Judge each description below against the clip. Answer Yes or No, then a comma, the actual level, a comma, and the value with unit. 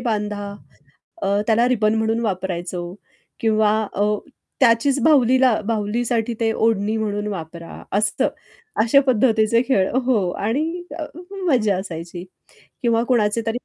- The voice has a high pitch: Yes, high, 220 Hz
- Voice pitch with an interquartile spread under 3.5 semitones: Yes, average, 2.7 semitones